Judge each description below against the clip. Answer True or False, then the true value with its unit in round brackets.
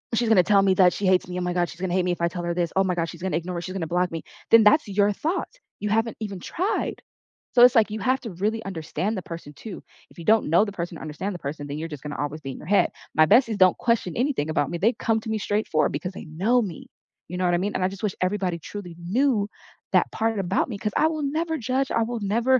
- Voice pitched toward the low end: False (190 Hz)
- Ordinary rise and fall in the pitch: True (4.4 semitones)